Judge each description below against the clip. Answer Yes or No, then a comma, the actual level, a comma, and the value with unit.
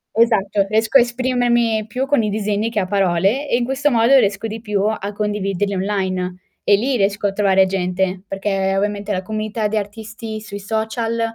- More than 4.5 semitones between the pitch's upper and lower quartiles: No, narrow, 2.5 semitones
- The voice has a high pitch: Yes, high, 210 Hz